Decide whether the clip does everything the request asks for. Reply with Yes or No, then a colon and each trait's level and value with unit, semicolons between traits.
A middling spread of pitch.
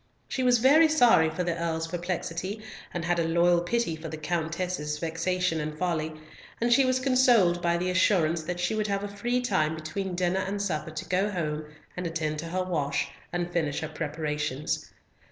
Yes: average, 3.7 semitones